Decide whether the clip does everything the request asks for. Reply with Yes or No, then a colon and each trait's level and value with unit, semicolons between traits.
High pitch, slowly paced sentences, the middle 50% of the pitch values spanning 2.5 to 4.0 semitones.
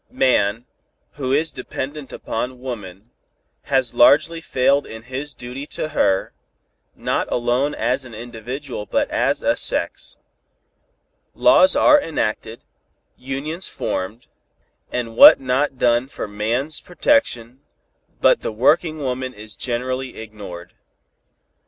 No: low, 125 Hz; slow, 120 wpm; average, 3.7 semitones